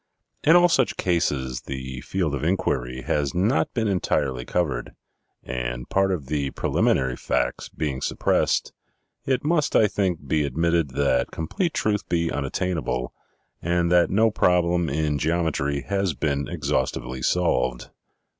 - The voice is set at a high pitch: No, very low, 80 Hz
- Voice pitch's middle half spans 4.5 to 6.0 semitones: Yes, wide, 5.4 semitones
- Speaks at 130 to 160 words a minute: Yes, slow, 135 wpm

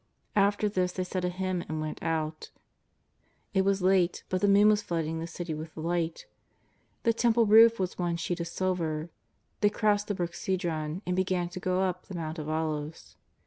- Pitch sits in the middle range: Yes, medium, 180 Hz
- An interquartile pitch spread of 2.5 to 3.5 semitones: Yes, average, 3.0 semitones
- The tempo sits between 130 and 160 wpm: No, average, 190 wpm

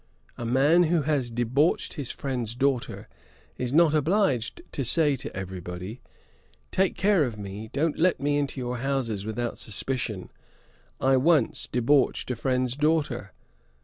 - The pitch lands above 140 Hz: No, low, 130 Hz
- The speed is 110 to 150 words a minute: Yes, average, 145 wpm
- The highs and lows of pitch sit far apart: No, average, 4.0 semitones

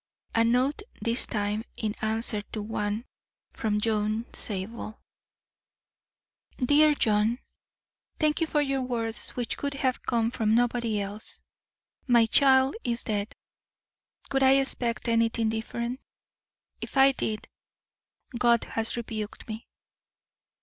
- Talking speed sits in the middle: No, slow, 115 wpm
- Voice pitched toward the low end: No, high, 230 Hz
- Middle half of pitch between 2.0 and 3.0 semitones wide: Yes, average, 2.7 semitones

